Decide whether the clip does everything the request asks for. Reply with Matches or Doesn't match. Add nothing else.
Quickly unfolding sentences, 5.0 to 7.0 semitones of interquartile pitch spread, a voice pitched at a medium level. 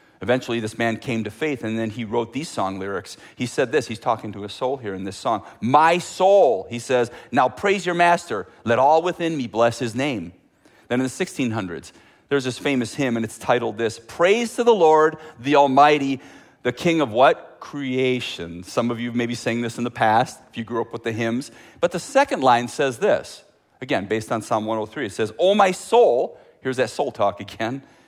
Doesn't match